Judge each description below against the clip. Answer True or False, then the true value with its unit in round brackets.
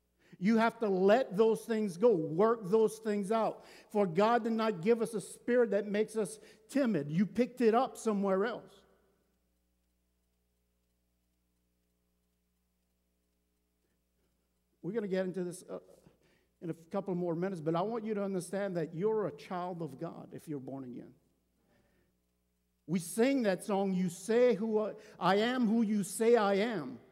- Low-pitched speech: False (190 Hz)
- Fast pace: False (155 wpm)